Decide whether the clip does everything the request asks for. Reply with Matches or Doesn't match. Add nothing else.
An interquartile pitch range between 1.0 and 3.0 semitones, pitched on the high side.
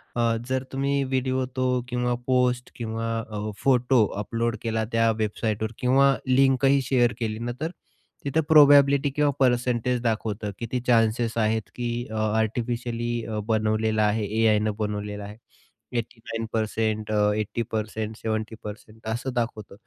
Doesn't match